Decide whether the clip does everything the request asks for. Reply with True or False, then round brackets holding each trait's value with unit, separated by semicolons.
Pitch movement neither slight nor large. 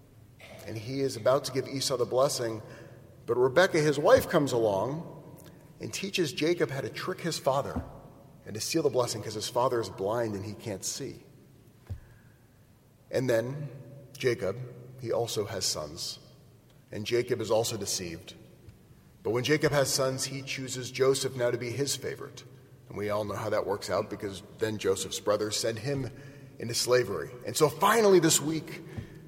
True (3.7 semitones)